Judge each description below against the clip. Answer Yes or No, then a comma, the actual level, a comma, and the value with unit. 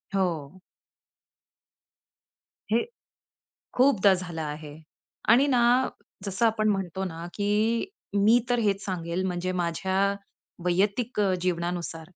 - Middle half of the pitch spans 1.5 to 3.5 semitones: No, average, 4.1 semitones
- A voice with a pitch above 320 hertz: No, high, 190 Hz